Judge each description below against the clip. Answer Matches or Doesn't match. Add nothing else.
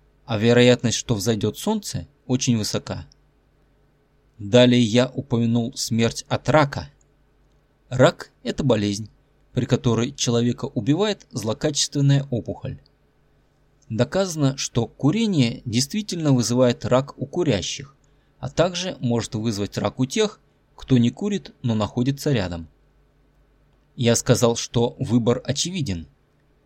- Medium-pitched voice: Doesn't match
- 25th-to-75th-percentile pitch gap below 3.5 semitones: Matches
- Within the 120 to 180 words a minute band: Doesn't match